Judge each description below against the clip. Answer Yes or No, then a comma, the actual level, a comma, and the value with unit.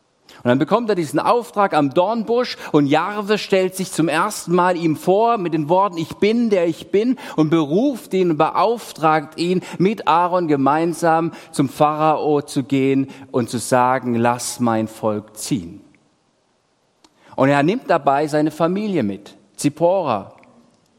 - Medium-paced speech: Yes, average, 150 wpm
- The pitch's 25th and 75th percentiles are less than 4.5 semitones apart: No, average, 5.1 semitones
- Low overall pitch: No, medium, 160 Hz